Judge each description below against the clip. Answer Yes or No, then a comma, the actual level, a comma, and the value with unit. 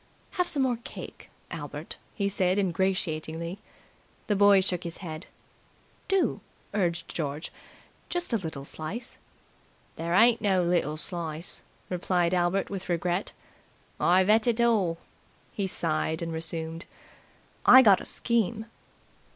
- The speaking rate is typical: No, slow, 125 wpm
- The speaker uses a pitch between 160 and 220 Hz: Yes, medium, 185 Hz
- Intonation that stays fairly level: No, average, 3.8 semitones